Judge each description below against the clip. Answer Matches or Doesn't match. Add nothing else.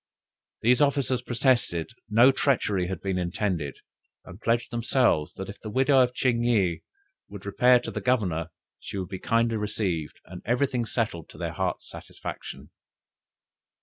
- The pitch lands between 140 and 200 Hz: Doesn't match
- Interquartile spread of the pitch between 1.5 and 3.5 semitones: Doesn't match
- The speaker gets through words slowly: Doesn't match